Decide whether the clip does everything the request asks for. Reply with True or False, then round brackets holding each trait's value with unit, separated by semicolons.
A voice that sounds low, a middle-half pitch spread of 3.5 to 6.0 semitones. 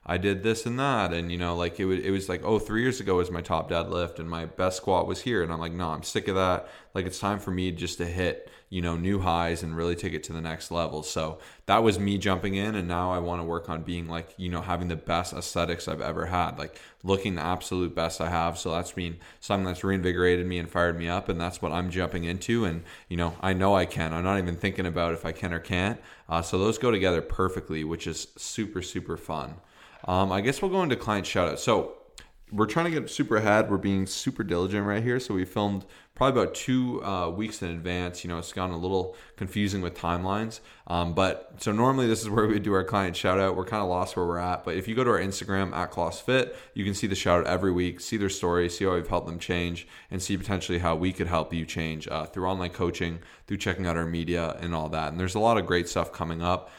False (90 Hz; 2.5 semitones)